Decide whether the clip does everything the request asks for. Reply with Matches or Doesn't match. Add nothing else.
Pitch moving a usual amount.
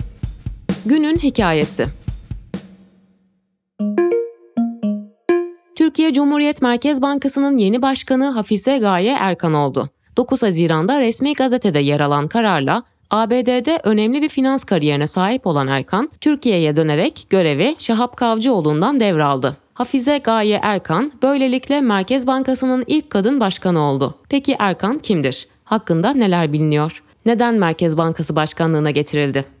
Doesn't match